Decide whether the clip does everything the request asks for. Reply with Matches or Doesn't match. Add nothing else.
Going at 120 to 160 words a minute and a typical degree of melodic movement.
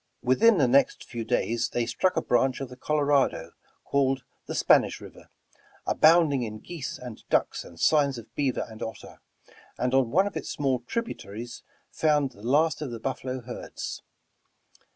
Doesn't match